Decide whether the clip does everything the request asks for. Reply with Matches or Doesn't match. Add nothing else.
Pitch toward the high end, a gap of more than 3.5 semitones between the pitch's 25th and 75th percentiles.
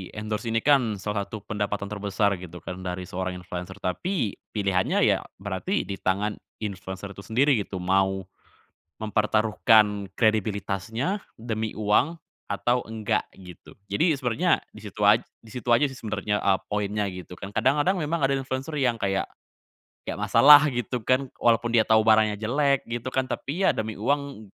Doesn't match